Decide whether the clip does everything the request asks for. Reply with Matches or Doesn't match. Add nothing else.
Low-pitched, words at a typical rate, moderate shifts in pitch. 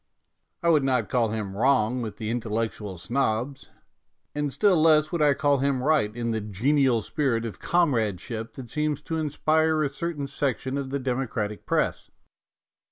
Matches